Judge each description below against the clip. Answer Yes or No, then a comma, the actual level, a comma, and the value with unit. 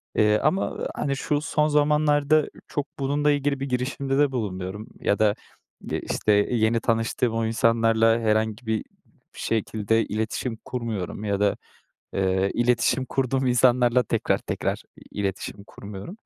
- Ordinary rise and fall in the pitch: Yes, average, 4.1 semitones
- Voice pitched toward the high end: No, low, 115 Hz